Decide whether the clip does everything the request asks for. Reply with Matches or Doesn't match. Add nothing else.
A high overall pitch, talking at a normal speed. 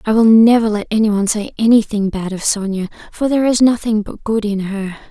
Doesn't match